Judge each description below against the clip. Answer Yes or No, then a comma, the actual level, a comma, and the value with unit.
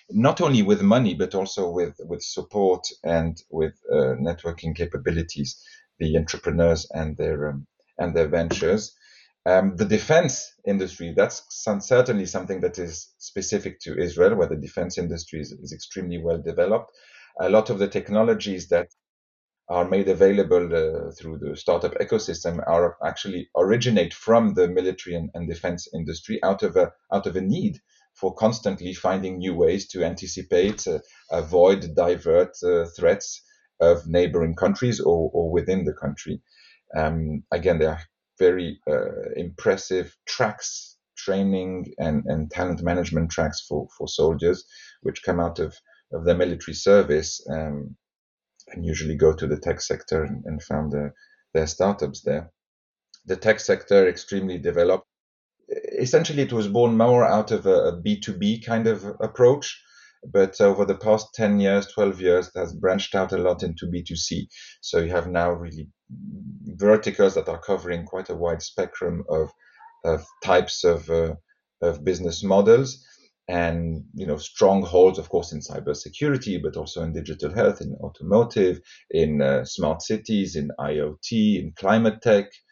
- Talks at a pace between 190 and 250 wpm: No, average, 155 wpm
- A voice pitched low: Yes, very low, 95 Hz